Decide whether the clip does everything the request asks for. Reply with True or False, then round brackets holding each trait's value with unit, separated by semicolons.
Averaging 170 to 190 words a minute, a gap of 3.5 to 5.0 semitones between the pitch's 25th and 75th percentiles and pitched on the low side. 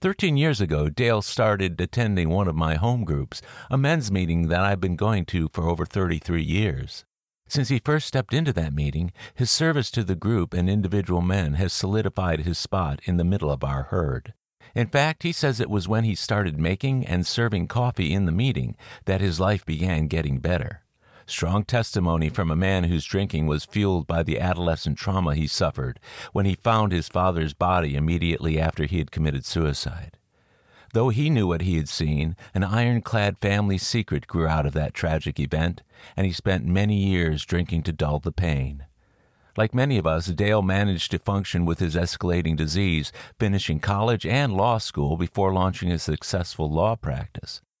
True (185 wpm; 4.6 semitones; 90 Hz)